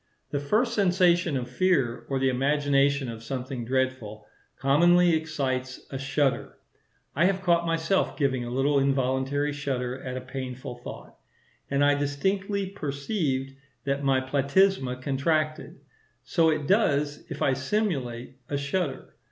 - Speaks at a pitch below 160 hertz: Yes, medium, 140 Hz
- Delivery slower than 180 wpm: Yes, slow, 135 wpm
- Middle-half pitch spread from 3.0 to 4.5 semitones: Yes, average, 3.8 semitones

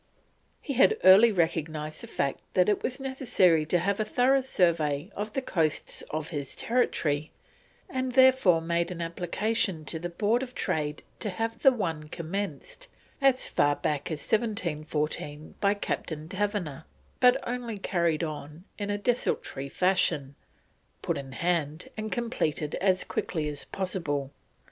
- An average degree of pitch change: No, wide, 6.2 semitones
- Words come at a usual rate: Yes, average, 150 wpm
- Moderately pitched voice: Yes, medium, 175 Hz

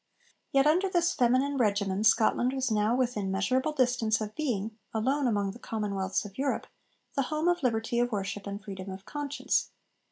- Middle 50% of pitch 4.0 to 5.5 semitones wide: Yes, average, 4.8 semitones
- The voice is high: Yes, high, 235 Hz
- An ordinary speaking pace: Yes, average, 170 wpm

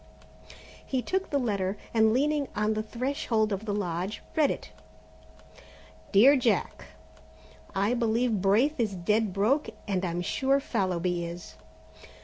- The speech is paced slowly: Yes, slow, 130 wpm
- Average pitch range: Yes, average, 4.7 semitones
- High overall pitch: Yes, high, 220 Hz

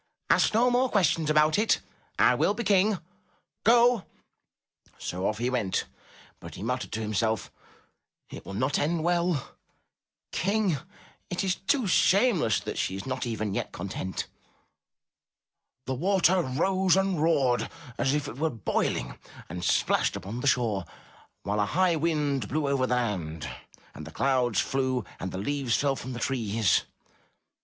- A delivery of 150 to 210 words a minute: Yes, average, 160 wpm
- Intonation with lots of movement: Yes, wide, 8.3 semitones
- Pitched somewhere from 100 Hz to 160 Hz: Yes, low, 135 Hz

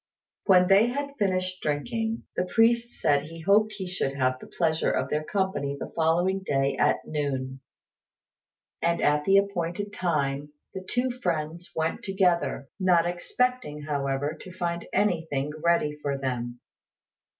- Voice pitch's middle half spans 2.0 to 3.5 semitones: No, average, 4.8 semitones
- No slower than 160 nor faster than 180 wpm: No, average, 145 wpm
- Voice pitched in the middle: Yes, medium, 170 Hz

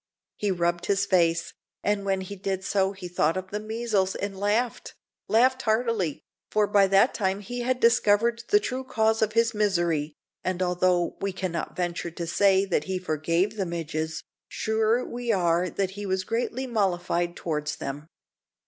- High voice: Yes, high, 195 Hz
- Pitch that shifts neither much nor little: Yes, average, 3.9 semitones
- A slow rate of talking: No, average, 170 wpm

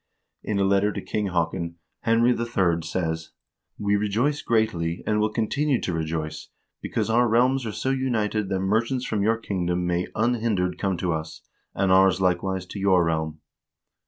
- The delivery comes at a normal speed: Yes, average, 170 wpm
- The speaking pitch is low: Yes, low, 100 Hz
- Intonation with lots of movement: No, average, 4.3 semitones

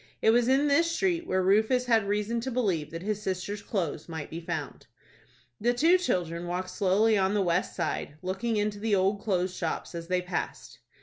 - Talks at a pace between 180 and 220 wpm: Yes, average, 195 wpm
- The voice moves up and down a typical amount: Yes, average, 4.3 semitones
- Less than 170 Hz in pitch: No, high, 200 Hz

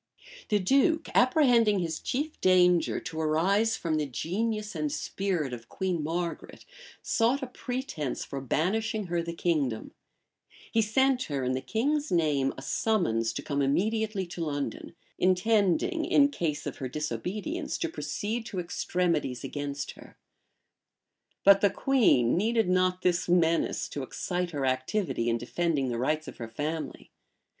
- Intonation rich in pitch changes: Yes, wide, 6.9 semitones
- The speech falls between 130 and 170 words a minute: Yes, average, 150 wpm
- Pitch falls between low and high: Yes, medium, 180 Hz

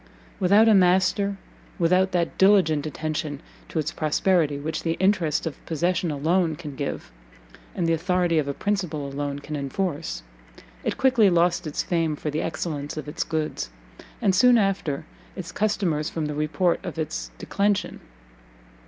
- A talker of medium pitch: Yes, medium, 165 Hz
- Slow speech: No, average, 155 wpm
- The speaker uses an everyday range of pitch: Yes, average, 3.7 semitones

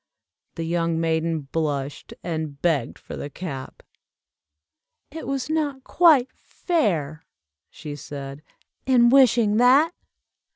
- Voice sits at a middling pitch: Yes, medium, 170 Hz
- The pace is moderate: No, slow, 110 wpm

